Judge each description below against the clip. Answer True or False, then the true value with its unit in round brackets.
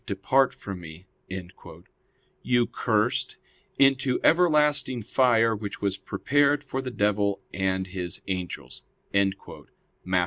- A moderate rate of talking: False (105 wpm)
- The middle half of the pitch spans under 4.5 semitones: False (5.6 semitones)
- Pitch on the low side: True (110 Hz)